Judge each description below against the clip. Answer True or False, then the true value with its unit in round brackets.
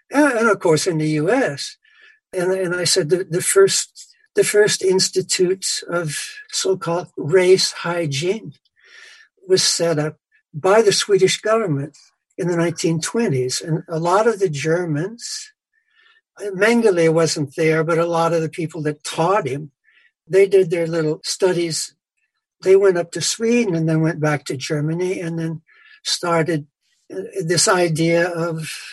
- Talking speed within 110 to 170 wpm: True (145 wpm)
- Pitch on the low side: False (180 Hz)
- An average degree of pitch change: False (6.0 semitones)